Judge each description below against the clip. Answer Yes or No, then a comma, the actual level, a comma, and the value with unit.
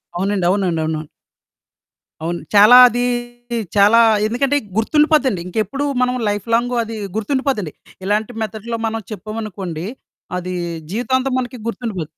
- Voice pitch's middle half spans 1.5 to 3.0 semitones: No, average, 4.3 semitones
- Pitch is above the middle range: Yes, high, 220 Hz